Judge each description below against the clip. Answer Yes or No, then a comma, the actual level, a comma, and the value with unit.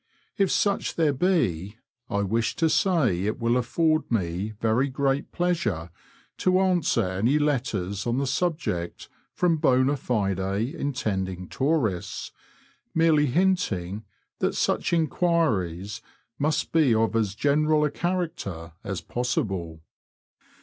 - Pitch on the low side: Yes, low, 125 Hz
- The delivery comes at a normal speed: No, slow, 125 wpm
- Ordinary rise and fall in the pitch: No, wide, 8.1 semitones